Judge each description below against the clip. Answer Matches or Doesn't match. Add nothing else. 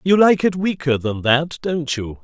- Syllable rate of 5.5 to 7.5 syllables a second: Doesn't match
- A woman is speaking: Doesn't match